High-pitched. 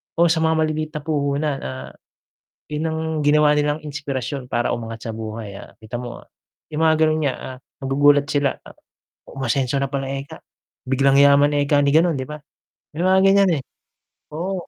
No: medium, 145 Hz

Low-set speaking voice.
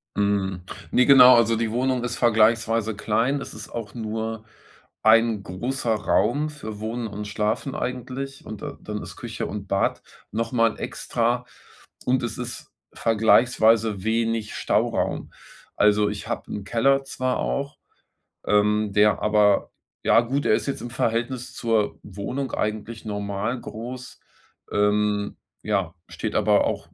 Yes: low, 115 Hz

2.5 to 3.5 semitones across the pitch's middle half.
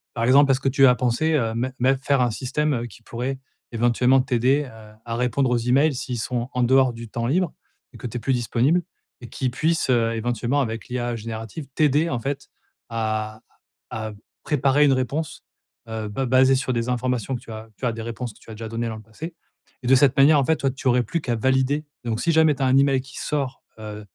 Yes: average, 2.8 semitones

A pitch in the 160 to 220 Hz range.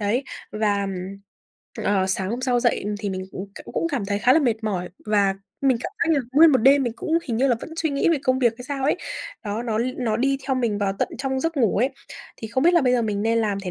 No: high, 235 Hz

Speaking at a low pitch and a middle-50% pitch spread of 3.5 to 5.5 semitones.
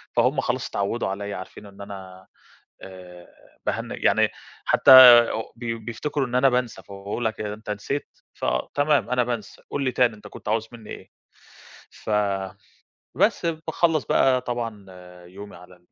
Yes: low, 110 Hz; average, 4.2 semitones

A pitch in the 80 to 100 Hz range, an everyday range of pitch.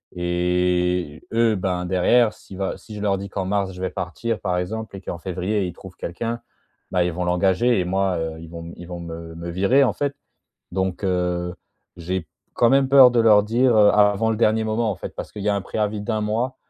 Yes: very low, 95 Hz; average, 3.4 semitones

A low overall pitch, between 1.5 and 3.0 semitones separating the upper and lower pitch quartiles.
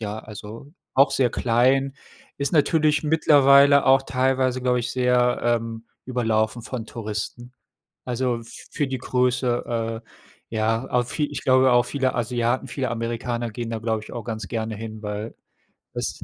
Yes: low, 120 Hz; narrow, 2.6 semitones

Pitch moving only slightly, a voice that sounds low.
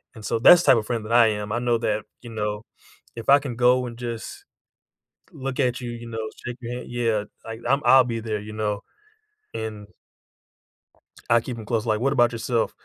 Yes: narrow, 2.1 semitones; low, 115 Hz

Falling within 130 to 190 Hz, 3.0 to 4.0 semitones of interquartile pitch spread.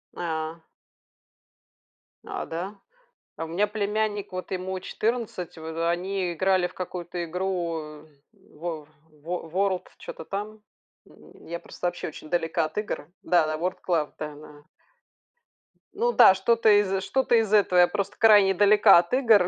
Yes: medium, 185 Hz; average, 3.7 semitones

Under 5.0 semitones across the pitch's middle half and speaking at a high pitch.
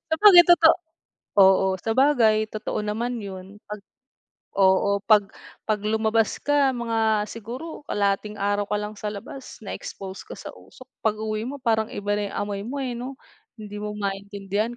Yes: average, 2.7 semitones; high, 215 Hz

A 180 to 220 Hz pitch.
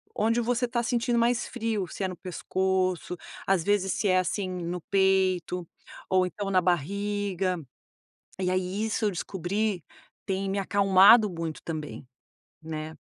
Yes: high, 190 Hz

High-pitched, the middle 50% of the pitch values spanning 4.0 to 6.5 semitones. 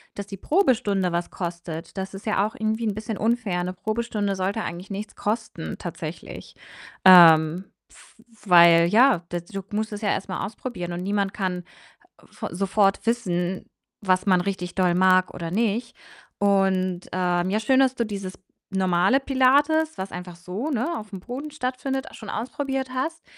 Yes: high, 200 Hz; average, 4.3 semitones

